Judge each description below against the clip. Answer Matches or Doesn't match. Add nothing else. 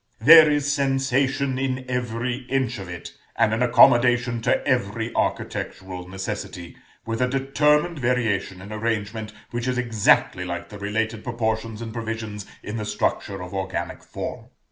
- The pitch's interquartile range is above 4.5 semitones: Doesn't match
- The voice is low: Matches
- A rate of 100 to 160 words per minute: Matches